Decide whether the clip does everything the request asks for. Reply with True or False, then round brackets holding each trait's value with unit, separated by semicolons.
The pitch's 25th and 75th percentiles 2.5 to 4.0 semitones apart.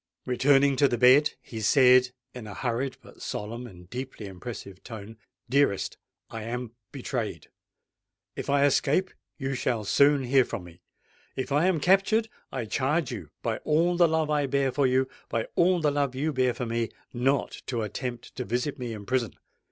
True (3.5 semitones)